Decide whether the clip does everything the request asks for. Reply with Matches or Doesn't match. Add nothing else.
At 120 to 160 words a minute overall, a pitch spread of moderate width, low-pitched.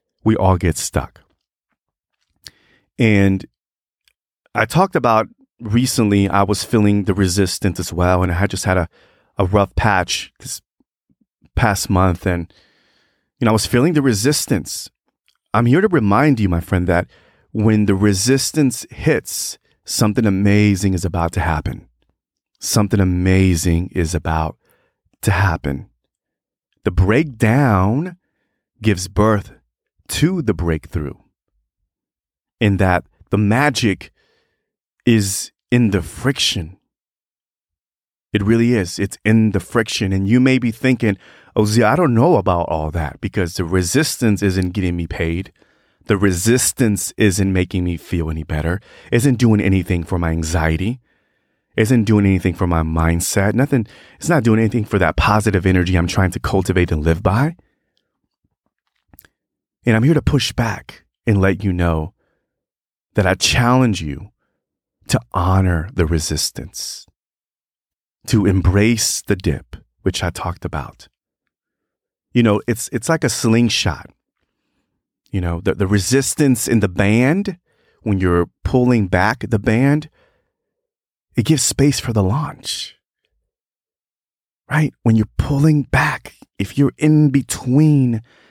Matches